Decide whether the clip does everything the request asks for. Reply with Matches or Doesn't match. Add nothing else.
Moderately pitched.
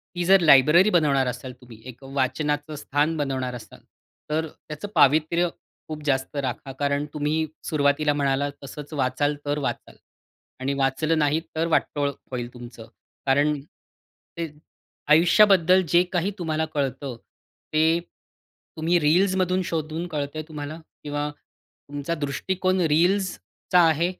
Matches